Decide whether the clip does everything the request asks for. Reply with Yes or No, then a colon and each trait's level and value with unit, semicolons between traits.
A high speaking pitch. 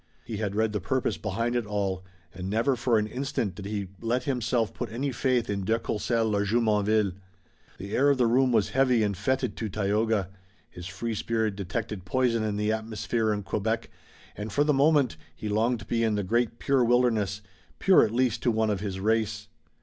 No: low, 110 Hz